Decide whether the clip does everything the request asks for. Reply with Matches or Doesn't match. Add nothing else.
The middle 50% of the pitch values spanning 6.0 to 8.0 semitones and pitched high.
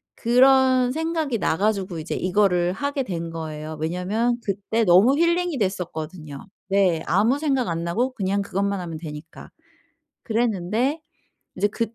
Matches